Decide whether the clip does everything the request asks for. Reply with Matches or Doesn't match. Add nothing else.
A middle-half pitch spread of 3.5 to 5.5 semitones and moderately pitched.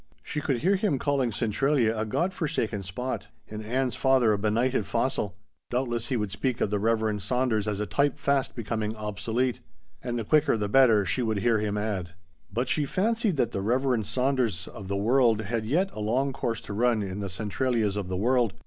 Doesn't match